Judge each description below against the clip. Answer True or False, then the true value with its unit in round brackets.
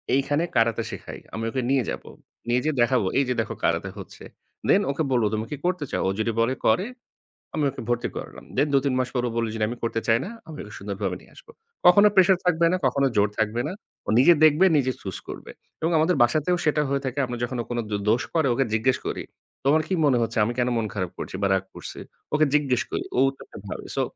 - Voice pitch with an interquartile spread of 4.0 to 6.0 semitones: True (4.8 semitones)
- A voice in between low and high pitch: False (130 Hz)